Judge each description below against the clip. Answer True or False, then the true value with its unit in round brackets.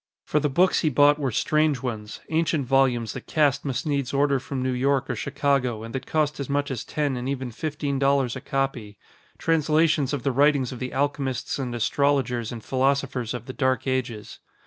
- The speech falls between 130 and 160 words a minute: False (195 wpm)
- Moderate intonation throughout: False (2.3 semitones)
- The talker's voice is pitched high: False (135 Hz)